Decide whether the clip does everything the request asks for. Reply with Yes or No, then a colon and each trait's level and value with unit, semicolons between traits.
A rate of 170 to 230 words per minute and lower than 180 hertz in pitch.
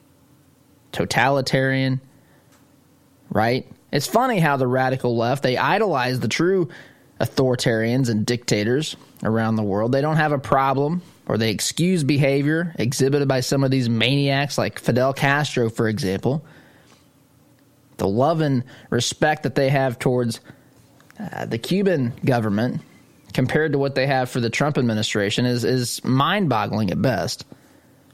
No: slow, 135 wpm; low, 135 Hz